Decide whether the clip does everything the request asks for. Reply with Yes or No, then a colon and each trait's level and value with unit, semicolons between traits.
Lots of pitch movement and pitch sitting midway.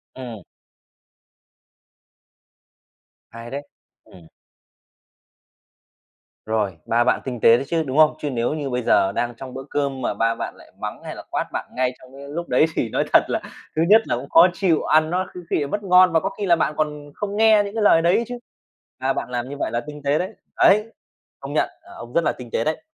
Yes: wide, 5.9 semitones; medium, 145 Hz